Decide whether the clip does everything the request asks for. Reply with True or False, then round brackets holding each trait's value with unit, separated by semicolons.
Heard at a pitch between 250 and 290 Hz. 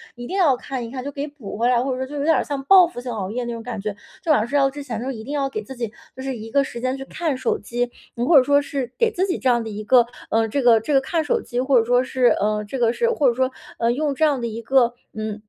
True (255 Hz)